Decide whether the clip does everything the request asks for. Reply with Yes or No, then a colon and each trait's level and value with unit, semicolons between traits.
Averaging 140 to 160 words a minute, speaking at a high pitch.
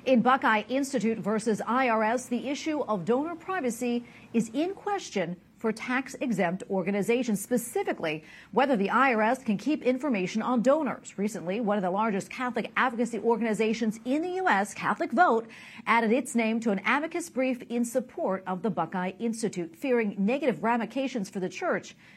Yes: average, 155 wpm; high, 235 Hz